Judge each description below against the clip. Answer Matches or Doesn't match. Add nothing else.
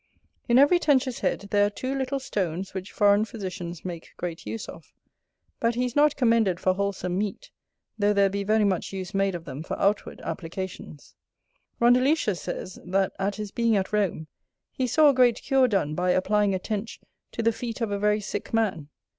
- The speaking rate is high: Doesn't match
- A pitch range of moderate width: Matches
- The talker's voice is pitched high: Matches